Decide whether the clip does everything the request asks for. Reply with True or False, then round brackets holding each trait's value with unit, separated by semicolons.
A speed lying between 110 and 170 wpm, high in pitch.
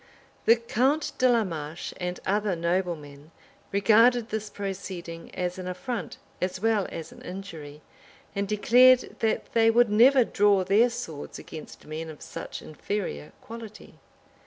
True (140 wpm; 200 Hz)